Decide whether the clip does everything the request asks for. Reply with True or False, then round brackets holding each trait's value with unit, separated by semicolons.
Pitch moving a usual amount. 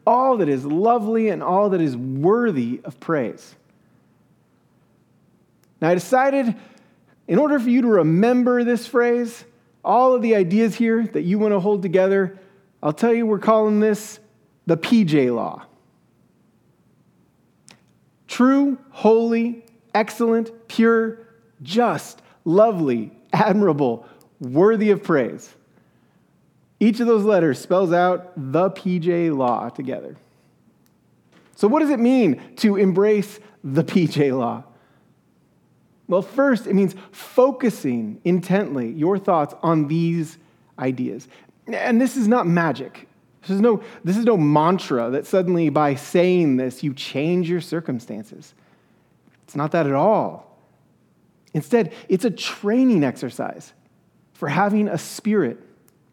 False (5.9 semitones)